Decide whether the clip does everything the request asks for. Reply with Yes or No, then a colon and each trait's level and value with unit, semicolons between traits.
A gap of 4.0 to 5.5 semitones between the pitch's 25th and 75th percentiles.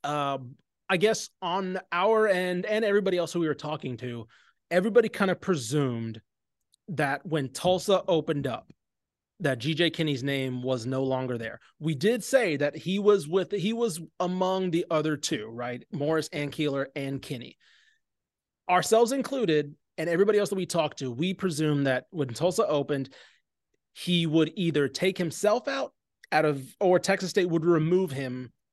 Yes: average, 4.8 semitones